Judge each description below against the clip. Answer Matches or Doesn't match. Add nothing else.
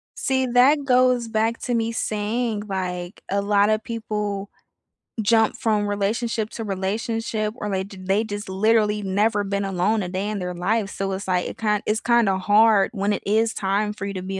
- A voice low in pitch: Doesn't match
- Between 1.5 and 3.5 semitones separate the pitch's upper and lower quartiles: Matches